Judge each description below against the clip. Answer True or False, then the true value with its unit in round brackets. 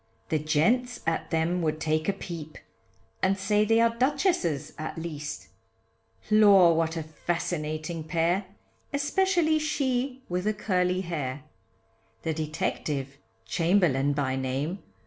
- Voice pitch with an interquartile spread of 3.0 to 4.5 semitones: False (5.5 semitones)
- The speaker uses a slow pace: True (125 wpm)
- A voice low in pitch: False (170 Hz)